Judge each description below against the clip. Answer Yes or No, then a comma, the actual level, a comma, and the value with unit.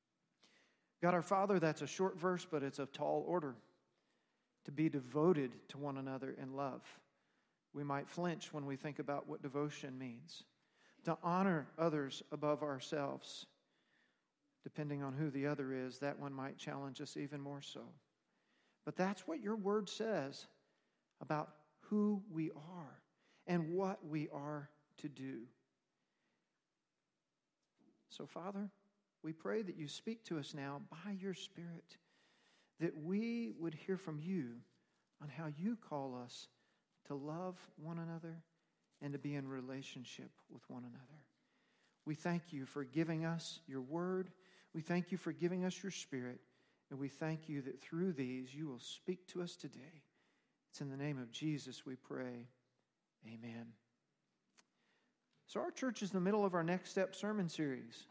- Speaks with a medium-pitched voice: Yes, medium, 155 Hz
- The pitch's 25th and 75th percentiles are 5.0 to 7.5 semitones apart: No, average, 4.6 semitones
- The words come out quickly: No, average, 155 wpm